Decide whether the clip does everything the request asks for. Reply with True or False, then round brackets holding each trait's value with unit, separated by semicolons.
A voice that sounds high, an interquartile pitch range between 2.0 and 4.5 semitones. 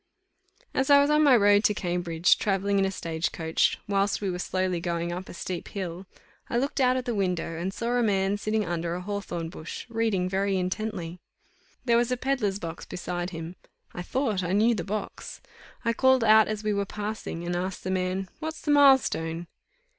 True (195 Hz; 4.0 semitones)